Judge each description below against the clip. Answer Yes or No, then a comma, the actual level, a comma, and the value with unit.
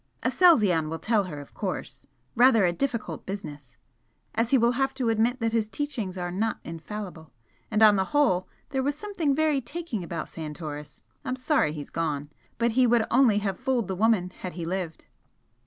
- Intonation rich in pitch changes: Yes, wide, 6.6 semitones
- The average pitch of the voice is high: Yes, high, 215 Hz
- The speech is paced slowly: No, average, 185 wpm